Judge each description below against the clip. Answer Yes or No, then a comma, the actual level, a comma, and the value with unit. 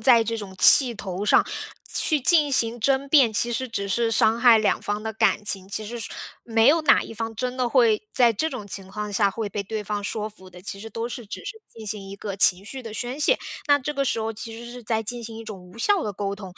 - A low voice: No, high, 225 Hz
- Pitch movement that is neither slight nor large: Yes, average, 3.0 semitones